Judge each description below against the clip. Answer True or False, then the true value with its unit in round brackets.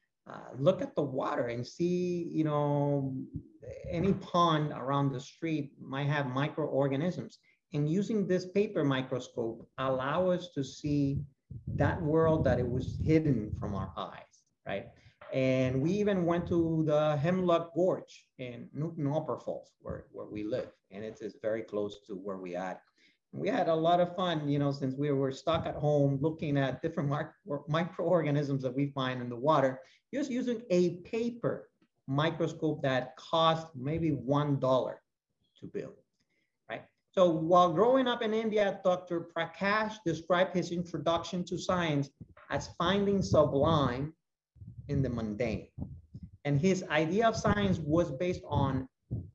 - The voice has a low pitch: False (150 Hz)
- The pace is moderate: True (155 wpm)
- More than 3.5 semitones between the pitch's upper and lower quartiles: True (4.7 semitones)